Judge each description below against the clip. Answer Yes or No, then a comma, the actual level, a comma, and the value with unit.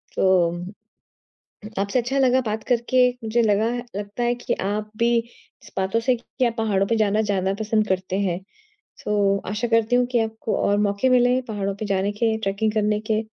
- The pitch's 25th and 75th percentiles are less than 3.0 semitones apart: Yes, narrow, 2.6 semitones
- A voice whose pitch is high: Yes, high, 215 Hz